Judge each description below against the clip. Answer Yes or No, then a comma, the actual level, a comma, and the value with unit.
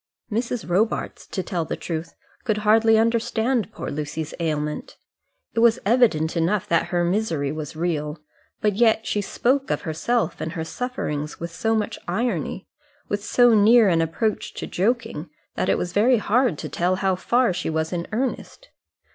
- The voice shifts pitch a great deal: Yes, wide, 5.7 semitones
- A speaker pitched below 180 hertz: No, high, 200 Hz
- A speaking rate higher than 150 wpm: Yes, average, 170 wpm